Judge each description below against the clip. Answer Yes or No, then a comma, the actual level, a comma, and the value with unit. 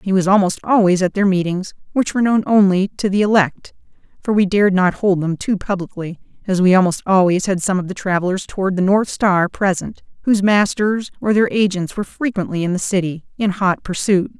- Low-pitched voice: No, high, 190 Hz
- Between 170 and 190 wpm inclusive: No, fast, 205 wpm